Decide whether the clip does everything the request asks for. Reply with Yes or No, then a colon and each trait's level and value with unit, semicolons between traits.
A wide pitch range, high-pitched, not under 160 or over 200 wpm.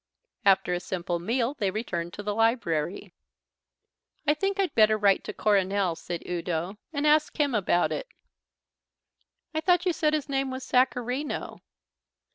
No: wide, 7.8 semitones; high, 225 Hz; average, 150 wpm